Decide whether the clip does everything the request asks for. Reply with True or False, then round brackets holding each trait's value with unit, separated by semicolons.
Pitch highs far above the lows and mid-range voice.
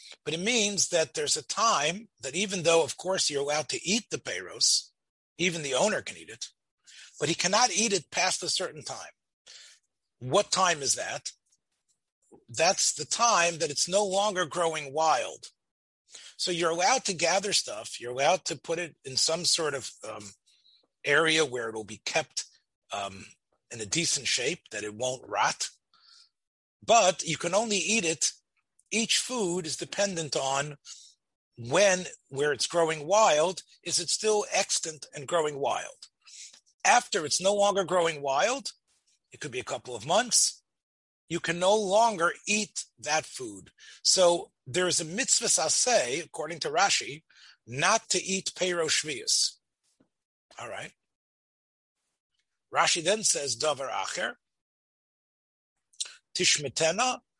False (5.0 semitones; 175 Hz)